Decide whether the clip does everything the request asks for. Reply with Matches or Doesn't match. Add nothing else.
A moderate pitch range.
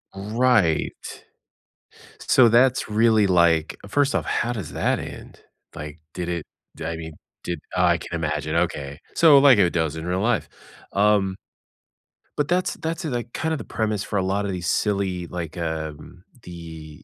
Doesn't match